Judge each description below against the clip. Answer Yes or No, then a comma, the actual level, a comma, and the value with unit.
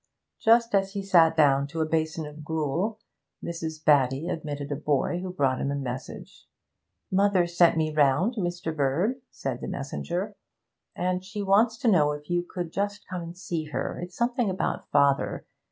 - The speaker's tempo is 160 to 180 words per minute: Yes, average, 175 wpm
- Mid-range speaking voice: Yes, medium, 165 Hz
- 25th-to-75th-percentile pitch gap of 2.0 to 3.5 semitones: No, average, 4.6 semitones